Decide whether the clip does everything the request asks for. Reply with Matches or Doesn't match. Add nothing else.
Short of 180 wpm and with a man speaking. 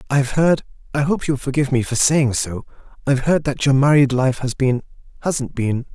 Matches